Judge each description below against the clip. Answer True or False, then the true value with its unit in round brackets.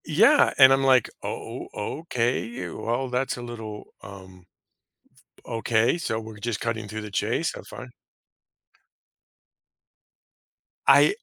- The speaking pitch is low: True (115 Hz)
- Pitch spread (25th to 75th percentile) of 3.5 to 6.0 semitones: False (2.9 semitones)